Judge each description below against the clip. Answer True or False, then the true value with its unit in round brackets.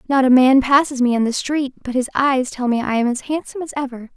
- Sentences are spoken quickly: True (275 wpm)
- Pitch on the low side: False (260 Hz)